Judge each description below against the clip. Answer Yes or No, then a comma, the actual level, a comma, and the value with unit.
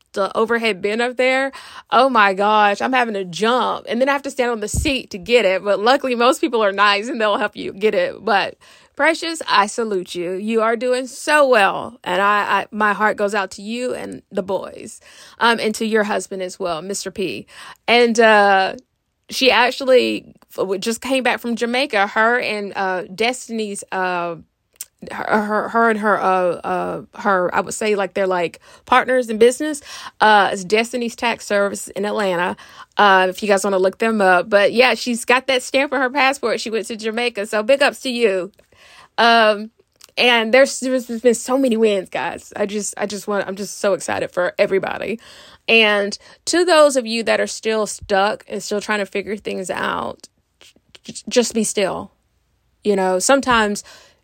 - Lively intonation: No, average, 3.7 semitones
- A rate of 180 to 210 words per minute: Yes, average, 195 wpm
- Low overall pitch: No, high, 220 Hz